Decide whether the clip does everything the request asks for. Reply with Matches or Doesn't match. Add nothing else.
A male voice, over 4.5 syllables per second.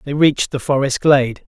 Matches